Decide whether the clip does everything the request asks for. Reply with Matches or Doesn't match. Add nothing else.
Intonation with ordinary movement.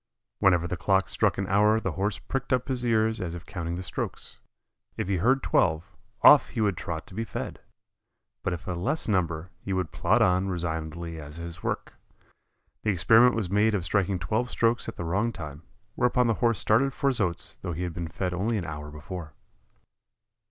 Matches